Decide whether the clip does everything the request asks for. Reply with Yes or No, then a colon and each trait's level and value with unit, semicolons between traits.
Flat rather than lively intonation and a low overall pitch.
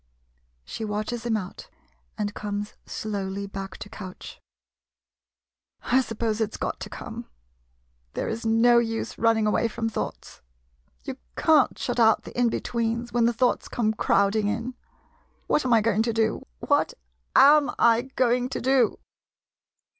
No: narrow, 2.2 semitones; high, 225 Hz